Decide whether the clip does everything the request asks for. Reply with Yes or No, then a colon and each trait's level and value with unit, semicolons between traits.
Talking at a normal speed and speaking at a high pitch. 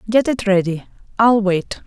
Yes: average, 160 wpm; high, 205 Hz